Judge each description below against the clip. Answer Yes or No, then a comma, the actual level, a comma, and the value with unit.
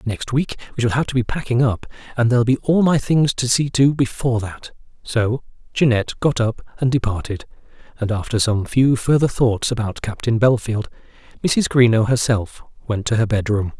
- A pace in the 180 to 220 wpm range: Yes, average, 185 wpm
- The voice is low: Yes, low, 120 Hz